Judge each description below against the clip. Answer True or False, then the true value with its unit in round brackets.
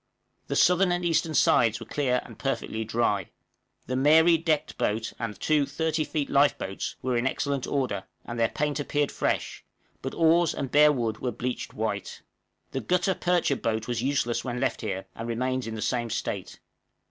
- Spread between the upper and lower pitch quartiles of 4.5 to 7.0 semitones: True (4.8 semitones)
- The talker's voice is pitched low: True (130 Hz)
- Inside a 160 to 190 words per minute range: True (180 wpm)